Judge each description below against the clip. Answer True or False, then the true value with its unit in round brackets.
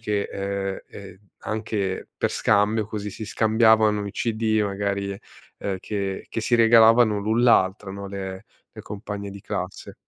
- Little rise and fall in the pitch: True (1.9 semitones)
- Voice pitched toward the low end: True (105 Hz)